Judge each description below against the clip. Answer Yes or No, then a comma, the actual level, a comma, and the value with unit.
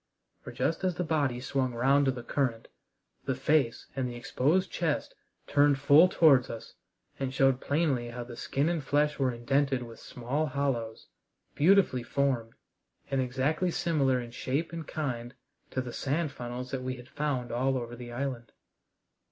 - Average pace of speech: Yes, average, 170 wpm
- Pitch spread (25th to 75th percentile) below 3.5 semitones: Yes, average, 3.0 semitones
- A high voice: No, low, 135 Hz